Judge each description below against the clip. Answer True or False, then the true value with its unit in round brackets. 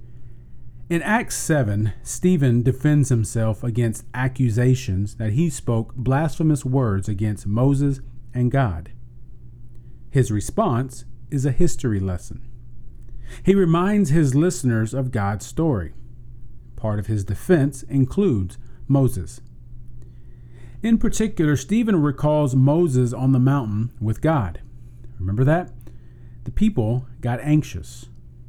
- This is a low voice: True (120 Hz)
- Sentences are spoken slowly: True (110 wpm)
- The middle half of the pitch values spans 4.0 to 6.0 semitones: False (3.1 semitones)